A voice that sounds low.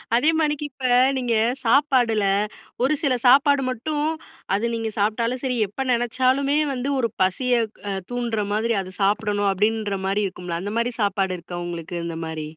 No: high, 230 Hz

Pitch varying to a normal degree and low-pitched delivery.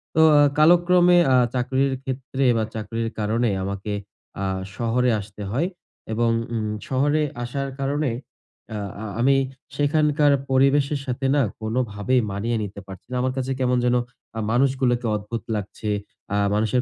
Yes: average, 3.7 semitones; low, 125 Hz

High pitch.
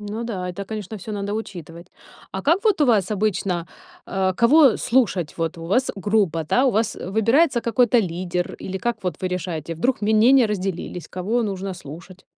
Yes: high, 200 Hz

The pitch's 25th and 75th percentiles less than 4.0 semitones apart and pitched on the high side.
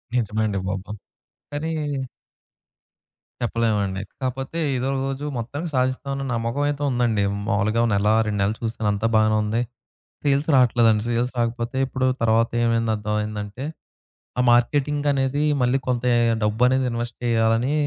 No: average, 3.2 semitones; low, 115 Hz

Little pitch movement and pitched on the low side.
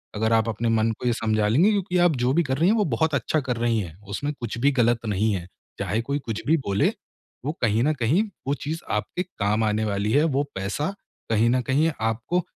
No: wide, 5.5 semitones; low, 120 Hz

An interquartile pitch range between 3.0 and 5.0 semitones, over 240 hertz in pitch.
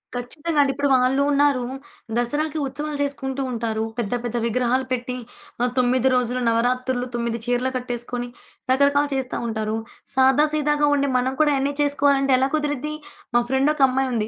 No: narrow, 2.5 semitones; very high, 260 Hz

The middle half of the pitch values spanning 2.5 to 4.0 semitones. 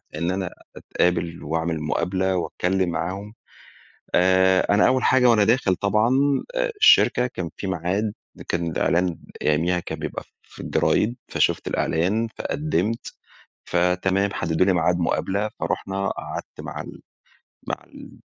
Yes: average, 2.8 semitones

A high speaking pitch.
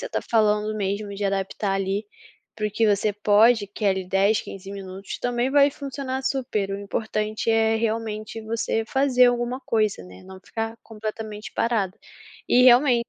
Yes: high, 215 Hz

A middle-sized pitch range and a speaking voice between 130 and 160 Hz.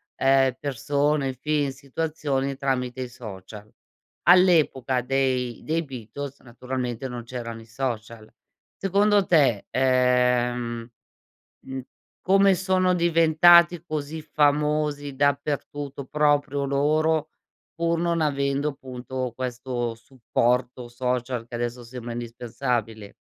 Yes: average, 3.5 semitones; low, 135 Hz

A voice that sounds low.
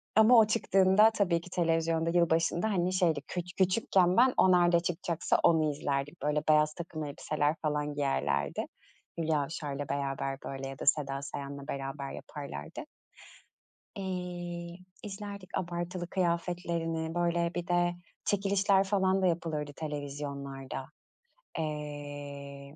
No: medium, 165 Hz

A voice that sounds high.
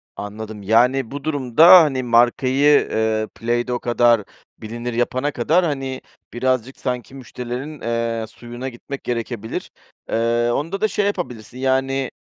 No: low, 125 Hz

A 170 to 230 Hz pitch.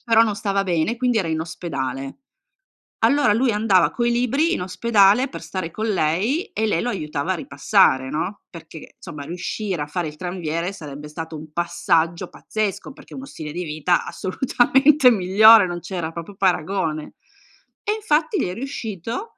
Yes: medium, 185 Hz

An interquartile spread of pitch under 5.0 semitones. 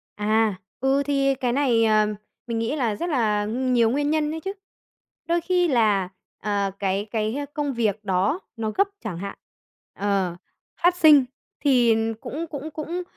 No: wide, 5.6 semitones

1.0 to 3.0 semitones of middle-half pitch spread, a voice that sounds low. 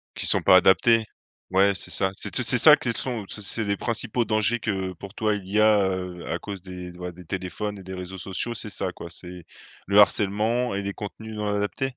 Yes: narrow, 2.6 semitones; low, 100 Hz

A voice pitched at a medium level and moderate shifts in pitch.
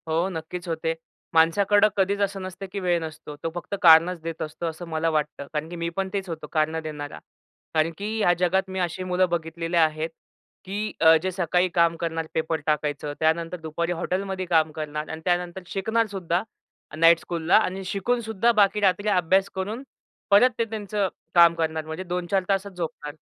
Yes: medium, 175 Hz; average, 3.1 semitones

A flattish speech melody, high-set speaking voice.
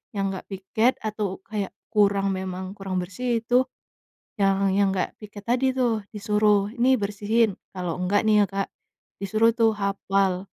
Yes: narrow, 2.0 semitones; high, 200 Hz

